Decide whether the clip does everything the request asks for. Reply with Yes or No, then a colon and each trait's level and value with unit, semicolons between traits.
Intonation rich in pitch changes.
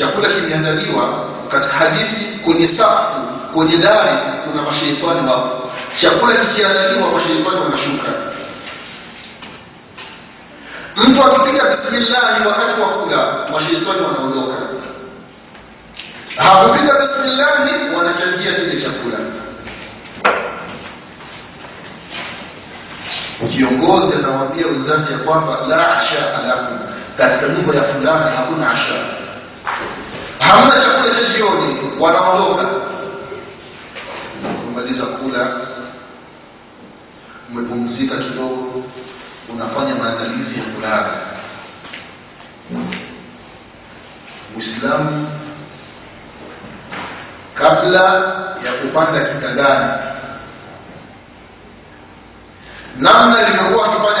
Yes: wide, 8.2 semitones